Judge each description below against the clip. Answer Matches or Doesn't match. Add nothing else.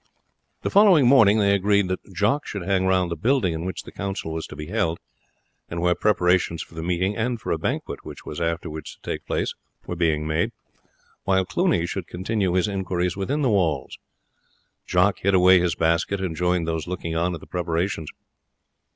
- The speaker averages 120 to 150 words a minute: Doesn't match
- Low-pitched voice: Matches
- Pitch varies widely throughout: Doesn't match